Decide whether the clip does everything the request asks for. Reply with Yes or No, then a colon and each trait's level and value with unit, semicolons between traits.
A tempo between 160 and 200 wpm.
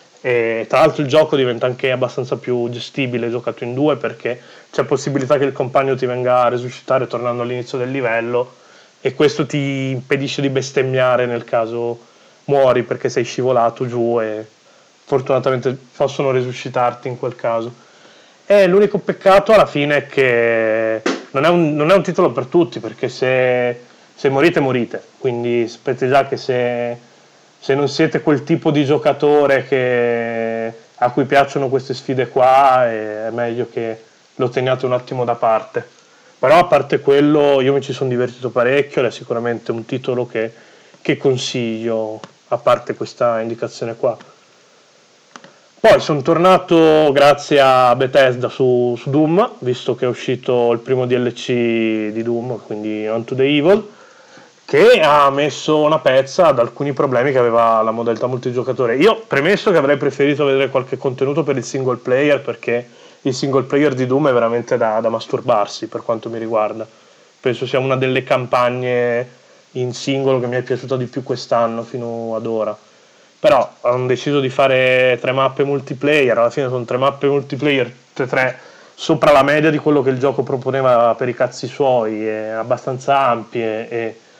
Yes: average, 165 wpm